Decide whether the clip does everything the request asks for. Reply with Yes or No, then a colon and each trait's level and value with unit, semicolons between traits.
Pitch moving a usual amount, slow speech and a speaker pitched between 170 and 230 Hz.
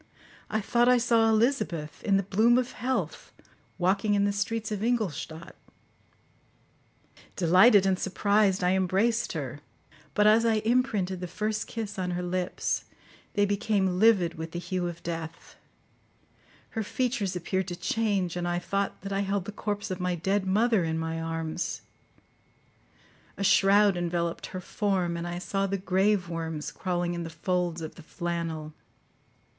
No: average, 3.3 semitones; average, 160 wpm; high, 190 Hz